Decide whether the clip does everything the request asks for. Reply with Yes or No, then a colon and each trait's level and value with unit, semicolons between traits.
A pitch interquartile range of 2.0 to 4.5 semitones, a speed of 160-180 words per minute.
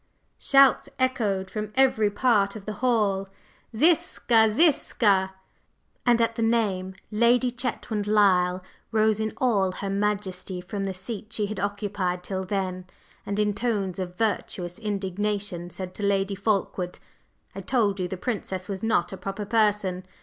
No: average, 2.7 semitones; average, 150 wpm